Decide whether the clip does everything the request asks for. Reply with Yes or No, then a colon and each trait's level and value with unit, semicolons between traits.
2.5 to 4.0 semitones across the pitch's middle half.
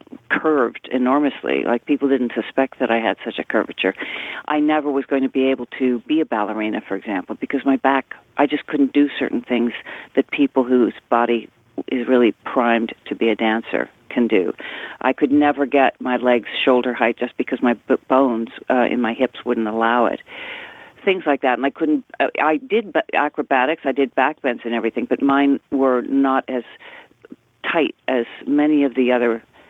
Yes: average, 2.9 semitones